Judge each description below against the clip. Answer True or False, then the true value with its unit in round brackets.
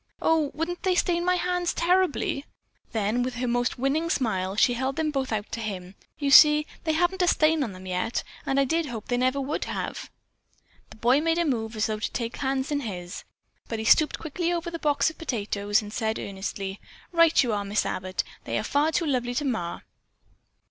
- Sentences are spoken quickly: True (215 wpm)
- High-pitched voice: True (265 Hz)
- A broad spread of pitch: True (6.6 semitones)